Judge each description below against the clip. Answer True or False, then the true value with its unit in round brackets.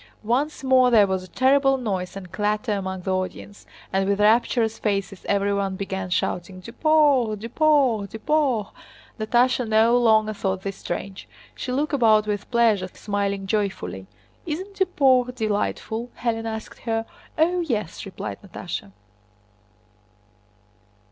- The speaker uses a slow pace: True (130 wpm)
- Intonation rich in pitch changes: False (4.2 semitones)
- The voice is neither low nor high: False (215 Hz)